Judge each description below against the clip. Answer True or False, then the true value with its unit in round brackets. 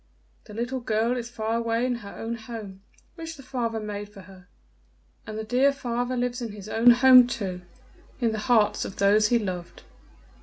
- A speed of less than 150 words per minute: False (190 wpm)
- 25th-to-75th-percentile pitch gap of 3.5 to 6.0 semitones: False (2.7 semitones)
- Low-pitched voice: False (230 Hz)